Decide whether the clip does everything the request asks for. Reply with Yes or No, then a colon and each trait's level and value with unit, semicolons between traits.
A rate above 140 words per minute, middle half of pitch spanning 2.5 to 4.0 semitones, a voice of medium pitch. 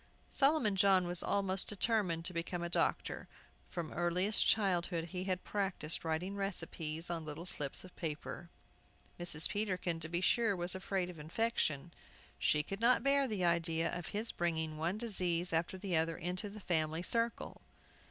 Yes: average, 160 wpm; average, 3.1 semitones; medium, 175 Hz